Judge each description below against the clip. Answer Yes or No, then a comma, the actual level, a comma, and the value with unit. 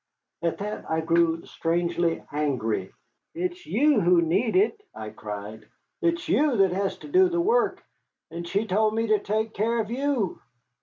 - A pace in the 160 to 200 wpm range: Yes, average, 165 wpm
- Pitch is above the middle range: Yes, high, 200 Hz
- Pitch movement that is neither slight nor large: No, wide, 8.7 semitones